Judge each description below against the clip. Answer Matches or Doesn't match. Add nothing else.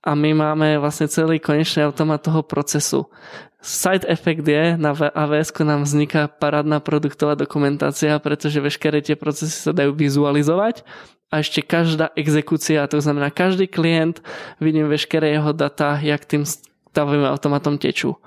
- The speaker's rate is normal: Matches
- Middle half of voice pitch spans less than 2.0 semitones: Matches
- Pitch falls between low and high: Matches